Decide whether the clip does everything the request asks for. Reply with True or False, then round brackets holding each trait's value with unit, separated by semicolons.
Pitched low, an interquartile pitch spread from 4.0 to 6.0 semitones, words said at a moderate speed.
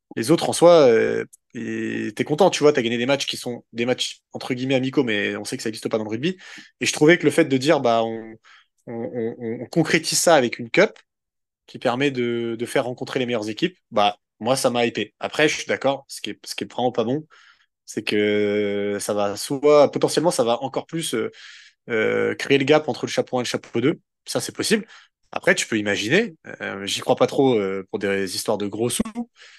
False (125 Hz; 5.2 semitones; 240 wpm)